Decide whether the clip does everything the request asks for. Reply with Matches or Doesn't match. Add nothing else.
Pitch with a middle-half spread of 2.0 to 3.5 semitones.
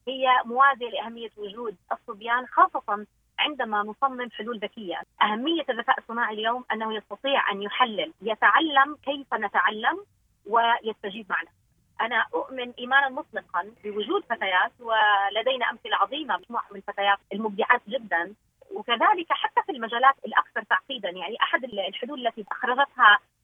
Doesn't match